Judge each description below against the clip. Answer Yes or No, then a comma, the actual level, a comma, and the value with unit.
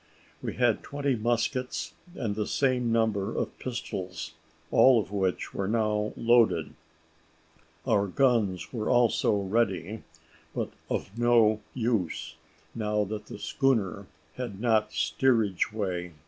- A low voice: Yes, low, 110 Hz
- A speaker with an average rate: No, slow, 120 wpm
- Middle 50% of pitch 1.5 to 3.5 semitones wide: Yes, average, 3.1 semitones